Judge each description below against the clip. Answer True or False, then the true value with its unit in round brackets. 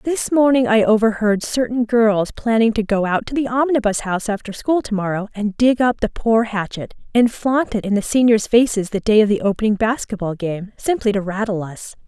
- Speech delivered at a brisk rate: True (210 wpm)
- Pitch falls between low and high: False (220 Hz)